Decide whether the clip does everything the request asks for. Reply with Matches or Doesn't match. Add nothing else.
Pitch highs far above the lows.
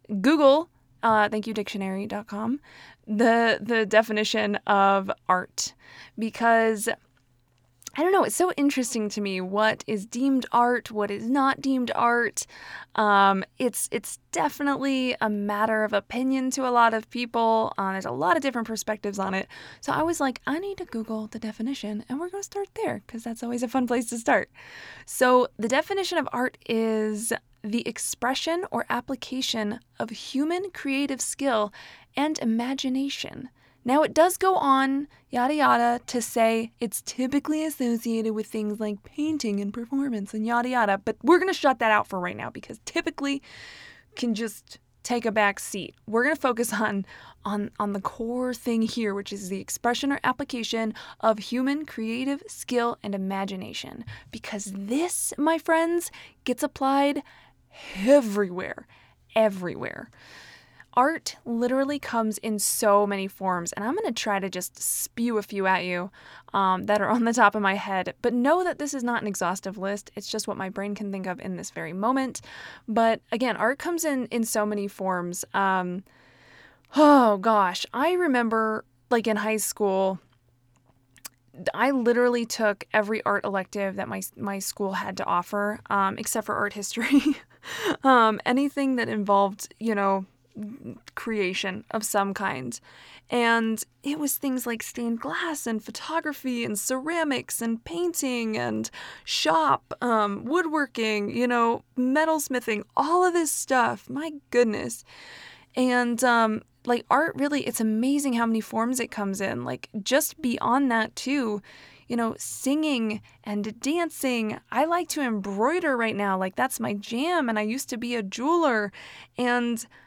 Doesn't match